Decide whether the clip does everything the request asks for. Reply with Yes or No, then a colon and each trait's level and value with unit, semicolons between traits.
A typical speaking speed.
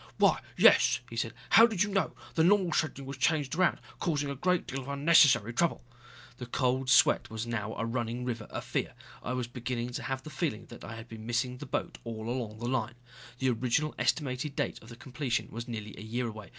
No: fast, 215 wpm